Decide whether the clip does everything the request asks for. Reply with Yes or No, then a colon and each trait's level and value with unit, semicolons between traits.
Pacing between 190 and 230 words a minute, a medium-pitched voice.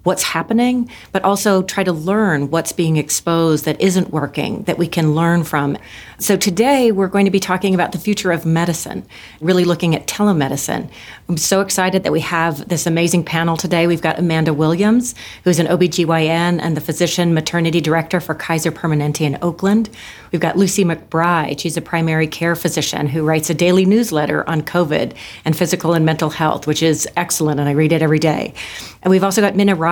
Yes: average, 195 wpm; medium, 170 Hz